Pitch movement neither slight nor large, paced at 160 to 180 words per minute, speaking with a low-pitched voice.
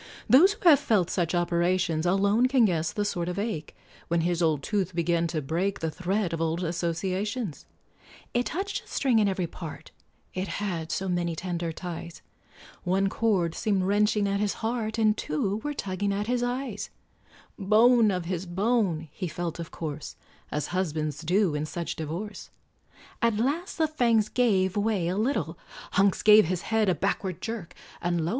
No: average, 4.1 semitones; average, 175 wpm; high, 190 Hz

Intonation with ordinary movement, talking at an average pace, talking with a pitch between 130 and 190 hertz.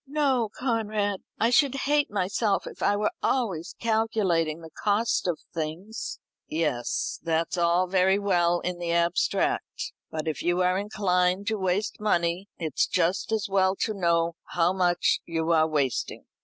Yes: average, 3.9 semitones; average, 155 wpm; medium, 185 Hz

